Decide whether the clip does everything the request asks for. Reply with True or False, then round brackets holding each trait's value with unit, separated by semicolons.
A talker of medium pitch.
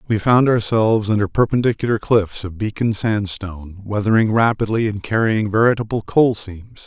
False (105 Hz)